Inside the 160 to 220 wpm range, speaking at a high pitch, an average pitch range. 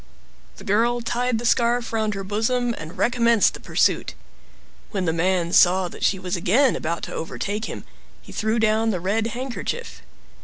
Yes: average, 170 wpm; high, 220 Hz; average, 4.1 semitones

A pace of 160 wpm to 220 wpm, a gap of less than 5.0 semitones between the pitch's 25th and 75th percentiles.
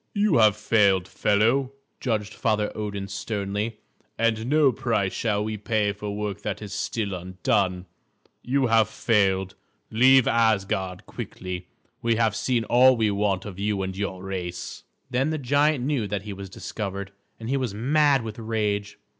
Yes: average, 165 wpm; average, 2.9 semitones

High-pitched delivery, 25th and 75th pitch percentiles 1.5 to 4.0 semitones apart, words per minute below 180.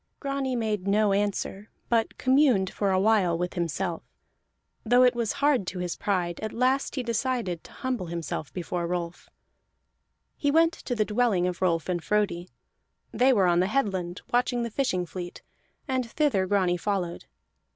No: high, 205 Hz; wide, 5.6 semitones; average, 165 wpm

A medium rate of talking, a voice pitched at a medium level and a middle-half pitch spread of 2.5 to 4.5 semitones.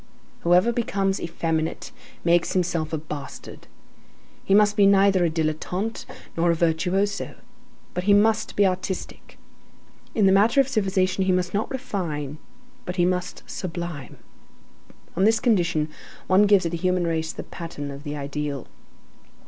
Yes: average, 150 wpm; medium, 180 Hz; average, 3.5 semitones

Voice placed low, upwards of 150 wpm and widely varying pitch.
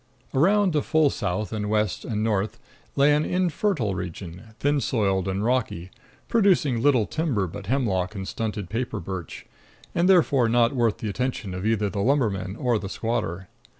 Yes: low, 110 Hz; average, 165 wpm; wide, 6.1 semitones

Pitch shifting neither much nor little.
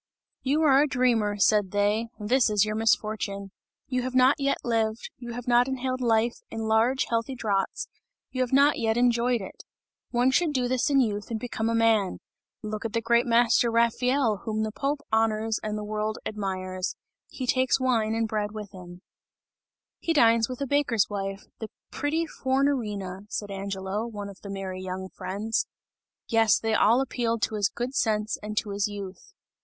Yes: average, 3.1 semitones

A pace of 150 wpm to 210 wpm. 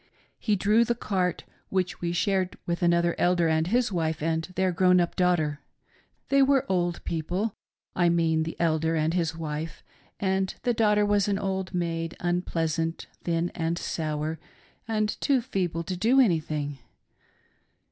Yes: average, 160 wpm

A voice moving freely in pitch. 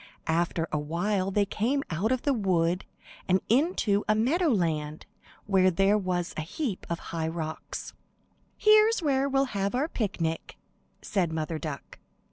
Yes: wide, 7.0 semitones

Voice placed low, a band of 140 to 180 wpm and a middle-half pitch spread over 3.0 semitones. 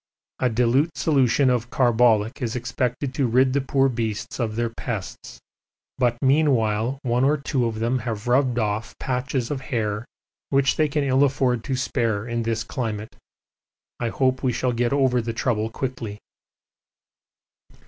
No: low, 125 Hz; average, 160 wpm; narrow, 2.5 semitones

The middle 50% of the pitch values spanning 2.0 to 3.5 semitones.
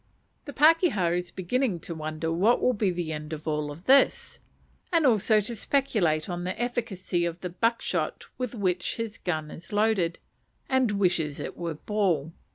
No: wide, 5.5 semitones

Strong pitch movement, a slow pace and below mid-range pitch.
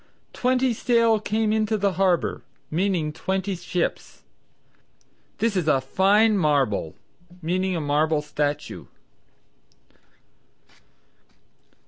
No: wide, 5.9 semitones; slow, 90 wpm; high, 190 Hz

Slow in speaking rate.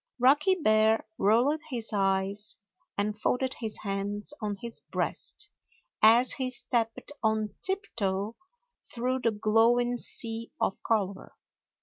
Yes: slow, 115 wpm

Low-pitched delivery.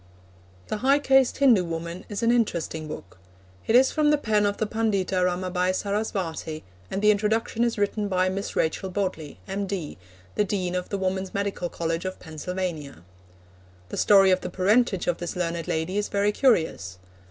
No: high, 190 Hz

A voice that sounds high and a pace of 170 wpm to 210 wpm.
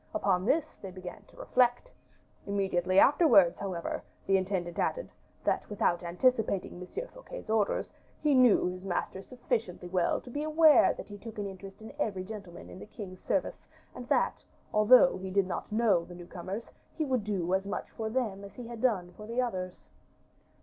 Yes: high, 200 Hz; average, 185 wpm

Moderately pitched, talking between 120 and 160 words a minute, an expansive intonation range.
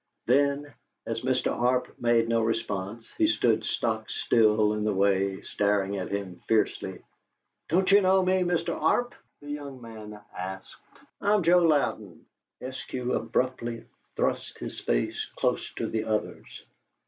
No: low, 115 Hz; average, 140 wpm; wide, 5.7 semitones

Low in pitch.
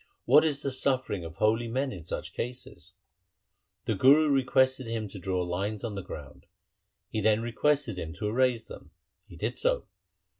Yes: low, 115 Hz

